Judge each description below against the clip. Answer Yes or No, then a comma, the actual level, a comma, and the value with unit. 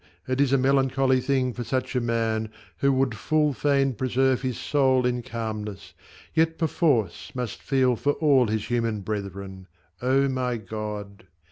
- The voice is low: Yes, low, 125 Hz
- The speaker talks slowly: No, average, 155 wpm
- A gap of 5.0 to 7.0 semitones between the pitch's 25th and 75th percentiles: No, average, 3.6 semitones